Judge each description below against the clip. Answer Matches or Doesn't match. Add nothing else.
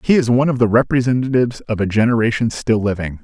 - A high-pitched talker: Doesn't match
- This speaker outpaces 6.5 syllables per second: Matches